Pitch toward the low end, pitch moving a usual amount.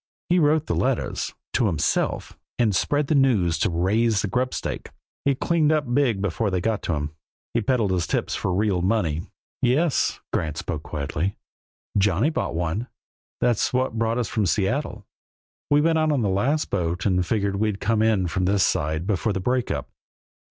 No: low, 105 Hz; wide, 5.7 semitones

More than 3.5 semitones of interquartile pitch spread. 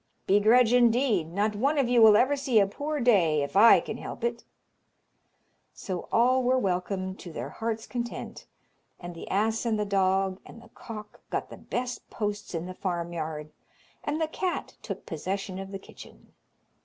Yes: average, 4.4 semitones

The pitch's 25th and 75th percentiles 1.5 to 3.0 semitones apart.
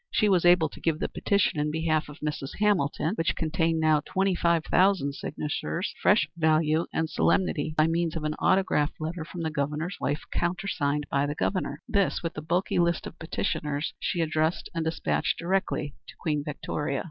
Yes: narrow, 2.6 semitones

